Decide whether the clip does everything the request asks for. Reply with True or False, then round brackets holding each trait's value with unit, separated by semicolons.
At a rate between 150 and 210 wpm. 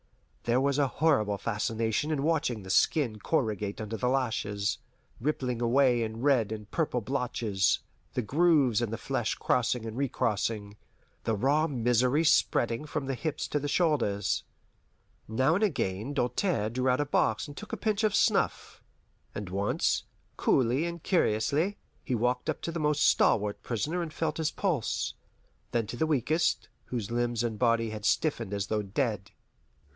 True (165 wpm)